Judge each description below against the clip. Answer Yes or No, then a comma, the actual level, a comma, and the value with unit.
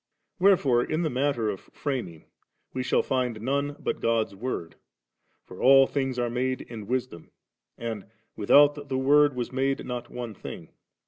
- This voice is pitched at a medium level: No, low, 130 Hz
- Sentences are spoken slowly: No, average, 165 wpm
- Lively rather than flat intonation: No, average, 3.2 semitones